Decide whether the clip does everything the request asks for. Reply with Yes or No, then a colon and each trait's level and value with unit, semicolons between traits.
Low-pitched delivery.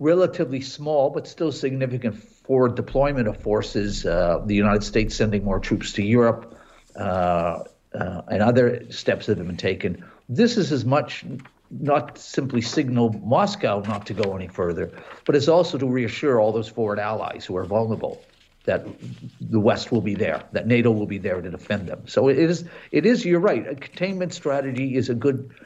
Yes: low, 120 Hz